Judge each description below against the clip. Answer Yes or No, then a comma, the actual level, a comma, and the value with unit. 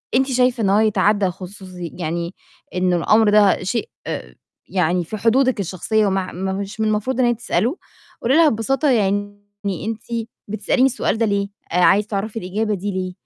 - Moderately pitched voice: No, high, 205 Hz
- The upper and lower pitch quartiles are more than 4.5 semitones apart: No, average, 3.3 semitones